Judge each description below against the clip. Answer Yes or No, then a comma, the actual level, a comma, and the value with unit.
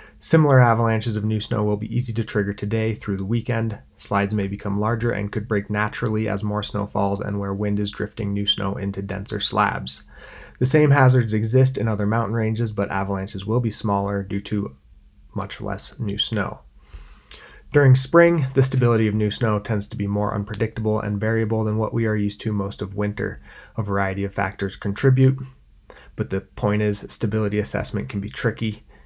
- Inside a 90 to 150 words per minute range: No, average, 190 wpm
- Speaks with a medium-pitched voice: No, low, 105 Hz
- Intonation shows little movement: Yes, narrow, 2.1 semitones